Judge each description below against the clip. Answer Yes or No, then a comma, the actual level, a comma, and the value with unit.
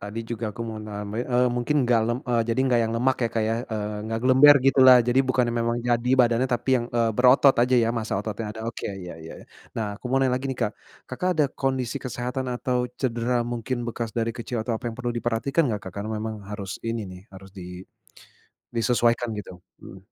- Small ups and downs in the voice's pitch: Yes, narrow, 2.2 semitones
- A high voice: No, low, 120 Hz